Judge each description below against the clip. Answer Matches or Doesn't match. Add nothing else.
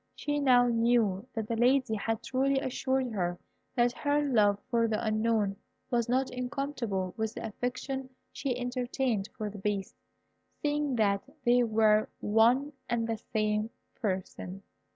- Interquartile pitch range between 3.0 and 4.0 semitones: Matches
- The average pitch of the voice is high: Matches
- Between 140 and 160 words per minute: Matches